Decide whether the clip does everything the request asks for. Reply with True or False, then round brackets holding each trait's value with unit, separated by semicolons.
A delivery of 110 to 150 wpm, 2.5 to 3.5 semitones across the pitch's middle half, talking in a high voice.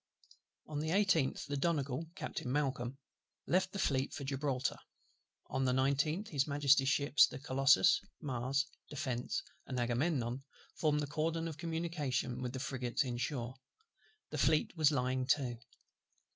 False (145 wpm; 3.1 semitones; 140 Hz)